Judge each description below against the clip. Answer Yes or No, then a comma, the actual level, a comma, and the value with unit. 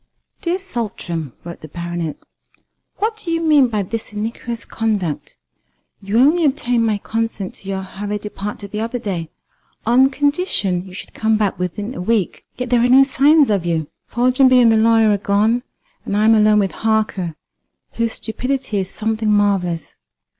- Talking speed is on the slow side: No, average, 170 wpm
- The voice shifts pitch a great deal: No, average, 4.0 semitones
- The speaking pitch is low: No, high, 220 Hz